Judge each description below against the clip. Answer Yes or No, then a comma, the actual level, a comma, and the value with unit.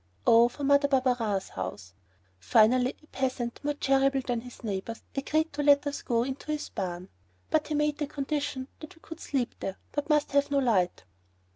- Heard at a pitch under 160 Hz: No, very high, 270 Hz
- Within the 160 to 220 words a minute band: Yes, average, 185 wpm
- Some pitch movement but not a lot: Yes, average, 4.0 semitones